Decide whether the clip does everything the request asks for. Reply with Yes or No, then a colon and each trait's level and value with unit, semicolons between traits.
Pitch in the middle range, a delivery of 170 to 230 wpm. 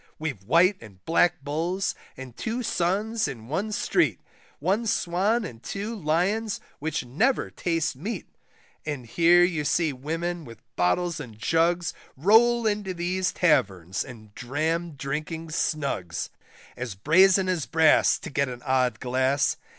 No: medium, 160 Hz; average, 140 wpm